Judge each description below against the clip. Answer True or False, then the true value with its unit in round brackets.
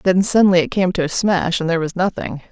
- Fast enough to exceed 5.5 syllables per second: True (5.8 syllables/s)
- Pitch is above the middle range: False (175 Hz)